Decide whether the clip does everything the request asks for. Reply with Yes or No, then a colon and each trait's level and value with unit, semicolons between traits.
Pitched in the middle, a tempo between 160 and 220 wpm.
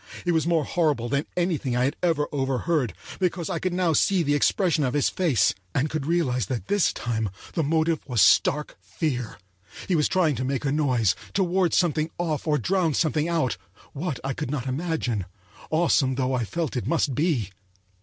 Yes: medium, 150 Hz; average, 190 wpm